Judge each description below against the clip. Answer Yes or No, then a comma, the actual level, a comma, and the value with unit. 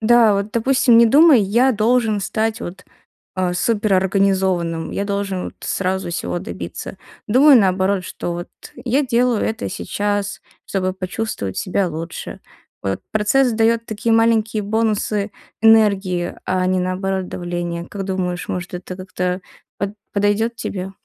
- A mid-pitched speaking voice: No, high, 200 Hz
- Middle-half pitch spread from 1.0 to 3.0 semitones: No, average, 3.4 semitones